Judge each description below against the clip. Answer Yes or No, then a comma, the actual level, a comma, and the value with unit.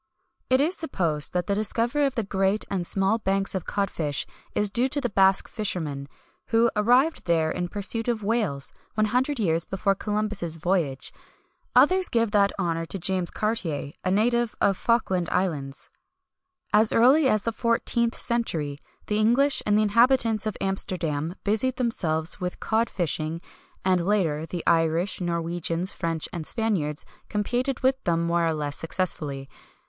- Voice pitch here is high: Yes, high, 195 Hz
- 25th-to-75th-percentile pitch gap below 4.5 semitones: No, wide, 5.4 semitones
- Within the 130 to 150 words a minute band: No, average, 165 wpm